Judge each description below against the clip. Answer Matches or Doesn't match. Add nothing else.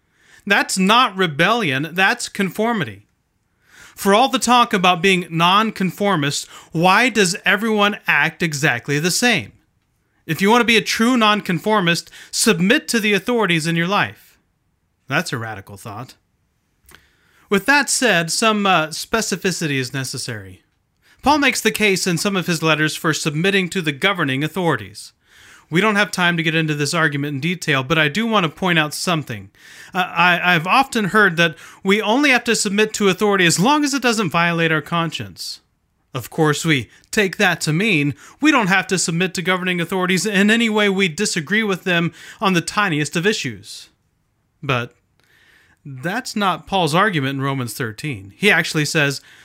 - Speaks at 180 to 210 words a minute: Doesn't match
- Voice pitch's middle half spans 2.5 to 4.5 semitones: Doesn't match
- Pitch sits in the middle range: Matches